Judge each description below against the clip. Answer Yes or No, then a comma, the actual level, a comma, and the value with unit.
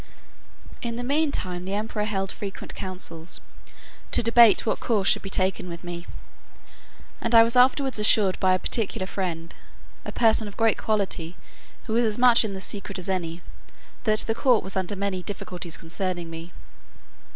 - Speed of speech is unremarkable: Yes, average, 175 wpm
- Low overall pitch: No, high, 200 Hz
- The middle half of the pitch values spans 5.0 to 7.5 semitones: No, average, 3.7 semitones